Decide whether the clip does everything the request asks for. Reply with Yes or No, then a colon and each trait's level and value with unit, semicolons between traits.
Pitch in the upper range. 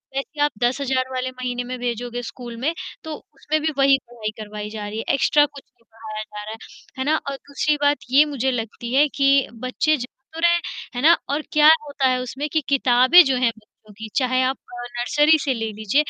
Yes: very high, 255 Hz